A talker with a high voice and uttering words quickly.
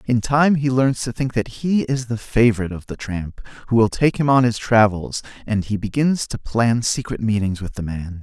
No: low, 115 Hz; fast, 225 wpm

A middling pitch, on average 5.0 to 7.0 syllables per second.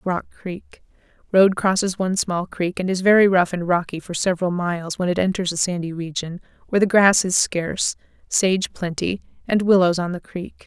Yes: medium, 180 Hz; 5.3 syllables/s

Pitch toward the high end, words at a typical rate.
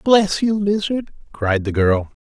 No: medium, 165 Hz; average, 160 wpm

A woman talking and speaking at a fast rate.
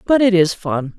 Yes: female; fast, 245 wpm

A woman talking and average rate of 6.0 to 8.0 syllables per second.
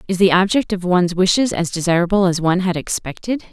Yes: female; 6.4 syllables/s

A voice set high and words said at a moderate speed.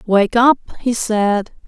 Yes: high, 225 Hz; average, 145 wpm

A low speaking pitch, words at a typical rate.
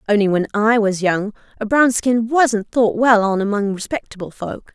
No: high, 215 Hz; average, 190 wpm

